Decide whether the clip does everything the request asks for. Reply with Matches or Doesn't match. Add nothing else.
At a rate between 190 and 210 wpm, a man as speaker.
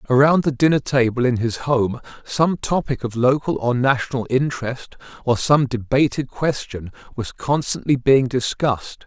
Doesn't match